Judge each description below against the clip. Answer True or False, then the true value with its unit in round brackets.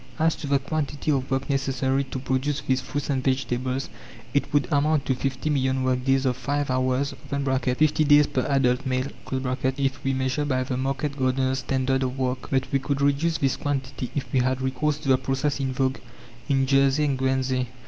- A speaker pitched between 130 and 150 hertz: True (135 Hz)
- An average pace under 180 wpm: False (195 wpm)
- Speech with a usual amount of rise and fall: False (1.4 semitones)